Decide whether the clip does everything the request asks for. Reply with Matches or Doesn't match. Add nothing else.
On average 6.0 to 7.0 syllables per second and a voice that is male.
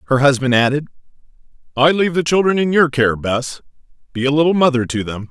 Matches